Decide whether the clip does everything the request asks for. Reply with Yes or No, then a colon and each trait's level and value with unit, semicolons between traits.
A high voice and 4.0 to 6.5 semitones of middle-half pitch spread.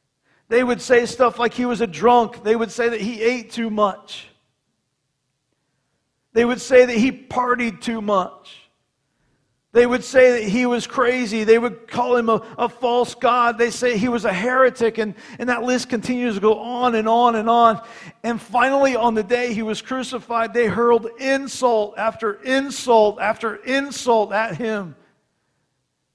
No: high, 230 Hz; average, 2.7 semitones